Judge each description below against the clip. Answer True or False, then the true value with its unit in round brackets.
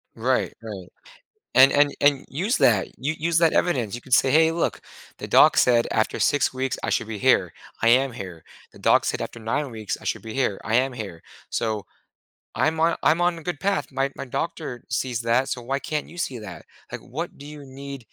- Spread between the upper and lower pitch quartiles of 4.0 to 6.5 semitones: True (4.6 semitones)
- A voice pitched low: True (130 Hz)